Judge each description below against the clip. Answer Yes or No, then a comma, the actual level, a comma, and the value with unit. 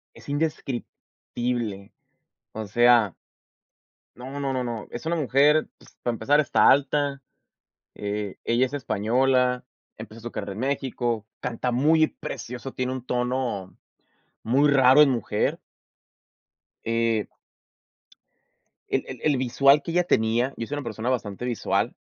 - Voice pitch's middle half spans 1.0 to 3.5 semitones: Yes, average, 3.2 semitones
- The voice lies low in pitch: Yes, low, 125 Hz